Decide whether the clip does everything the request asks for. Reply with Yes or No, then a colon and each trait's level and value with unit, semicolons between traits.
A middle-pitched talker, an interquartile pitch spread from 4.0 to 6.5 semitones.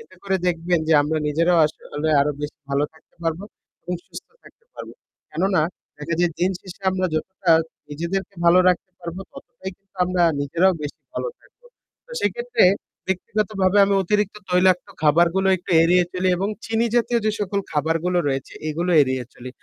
No: medium, 180 Hz; average, 3.0 semitones